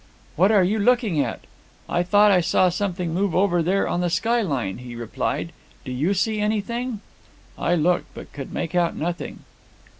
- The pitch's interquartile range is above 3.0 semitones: Yes, average, 3.9 semitones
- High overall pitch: No, medium, 180 Hz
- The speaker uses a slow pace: No, average, 175 wpm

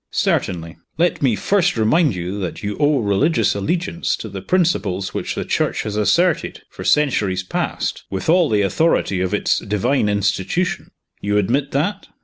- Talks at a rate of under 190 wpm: Yes, average, 160 wpm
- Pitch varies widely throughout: Yes, wide, 8.4 semitones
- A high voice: No, low, 105 Hz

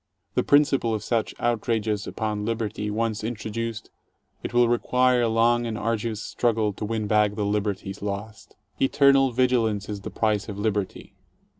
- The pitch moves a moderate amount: No, narrow, 2.2 semitones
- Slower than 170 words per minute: Yes, average, 155 wpm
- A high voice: No, low, 110 Hz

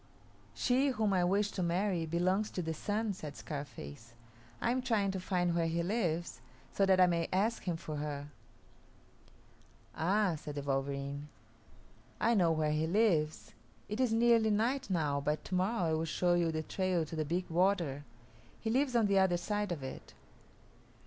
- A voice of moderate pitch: Yes, medium, 175 Hz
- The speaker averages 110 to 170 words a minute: No, average, 180 wpm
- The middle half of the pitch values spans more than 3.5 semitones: Yes, average, 4.7 semitones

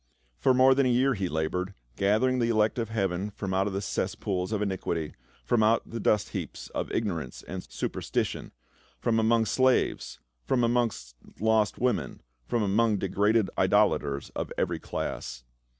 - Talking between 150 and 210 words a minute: Yes, average, 155 wpm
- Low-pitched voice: Yes, low, 105 Hz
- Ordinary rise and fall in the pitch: Yes, average, 3.6 semitones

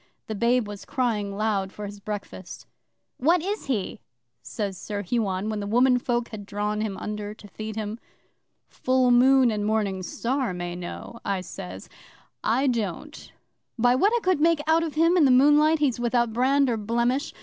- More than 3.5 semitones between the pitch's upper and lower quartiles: Yes, average, 4.2 semitones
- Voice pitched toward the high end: Yes, high, 230 Hz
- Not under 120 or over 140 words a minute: No, average, 175 wpm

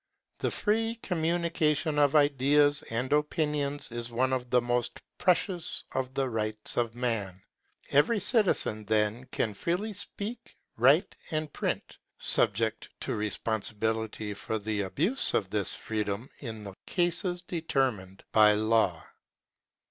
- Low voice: Yes, low, 125 Hz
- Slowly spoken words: Yes, slow, 125 wpm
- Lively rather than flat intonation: Yes, wide, 6.4 semitones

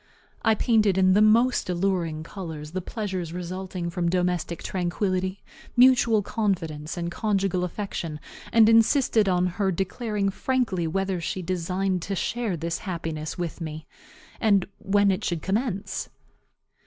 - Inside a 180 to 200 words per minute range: No, slow, 135 wpm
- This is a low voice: No, medium, 185 Hz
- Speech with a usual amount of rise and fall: Yes, average, 3.3 semitones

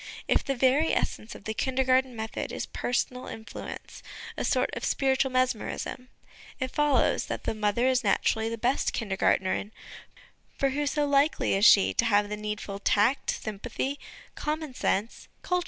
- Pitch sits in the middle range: No, very high, 250 Hz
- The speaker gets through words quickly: No, average, 155 wpm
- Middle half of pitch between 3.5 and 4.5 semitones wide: Yes, average, 4.2 semitones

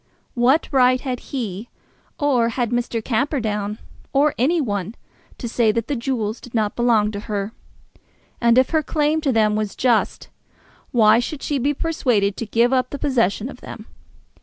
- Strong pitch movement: No, average, 3.8 semitones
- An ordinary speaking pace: Yes, average, 170 wpm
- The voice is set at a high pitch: Yes, high, 240 Hz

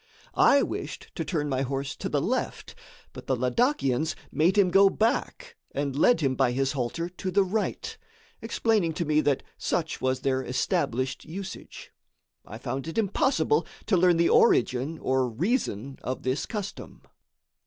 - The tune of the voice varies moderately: No, wide, 6.7 semitones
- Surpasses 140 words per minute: Yes, average, 160 wpm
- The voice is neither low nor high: Yes, medium, 155 Hz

